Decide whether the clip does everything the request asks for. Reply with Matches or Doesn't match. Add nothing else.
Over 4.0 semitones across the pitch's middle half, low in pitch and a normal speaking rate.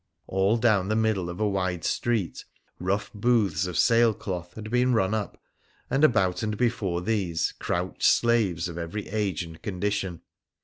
Doesn't match